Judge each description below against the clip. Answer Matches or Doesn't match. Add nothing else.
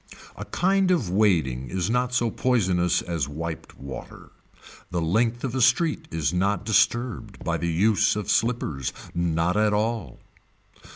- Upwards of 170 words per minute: Doesn't match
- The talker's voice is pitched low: Matches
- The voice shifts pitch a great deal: Matches